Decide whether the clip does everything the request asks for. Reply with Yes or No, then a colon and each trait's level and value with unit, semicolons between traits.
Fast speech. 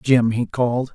No: average, 190 wpm